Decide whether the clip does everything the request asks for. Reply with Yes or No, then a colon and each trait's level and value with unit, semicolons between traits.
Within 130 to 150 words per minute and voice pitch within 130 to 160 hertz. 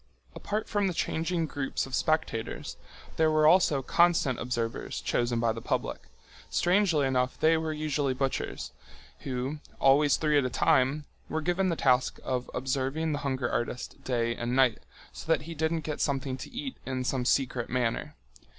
No: average, 160 wpm; medium, 140 Hz